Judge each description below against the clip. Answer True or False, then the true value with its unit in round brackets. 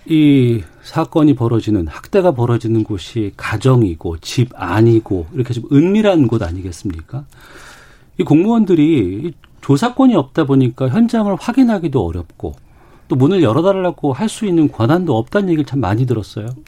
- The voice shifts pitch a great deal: True (7.3 semitones)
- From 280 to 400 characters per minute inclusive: True (335 characters per minute)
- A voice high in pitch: False (130 Hz)